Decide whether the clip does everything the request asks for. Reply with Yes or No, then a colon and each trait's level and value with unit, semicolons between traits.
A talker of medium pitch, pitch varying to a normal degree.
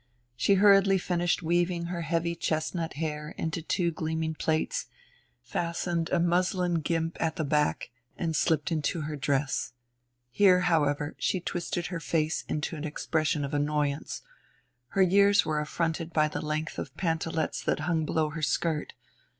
No: medium, 160 Hz; narrow, 2.2 semitones